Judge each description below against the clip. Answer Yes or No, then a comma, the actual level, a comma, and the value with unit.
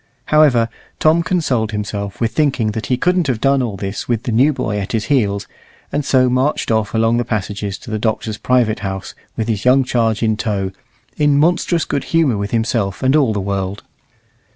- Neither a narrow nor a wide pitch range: Yes, average, 4.5 semitones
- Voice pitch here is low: Yes, low, 115 Hz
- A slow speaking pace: No, average, 200 wpm